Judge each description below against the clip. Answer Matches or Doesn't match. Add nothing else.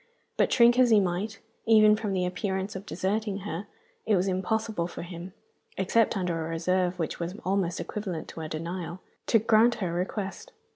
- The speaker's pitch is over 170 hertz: Matches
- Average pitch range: Matches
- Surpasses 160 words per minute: Matches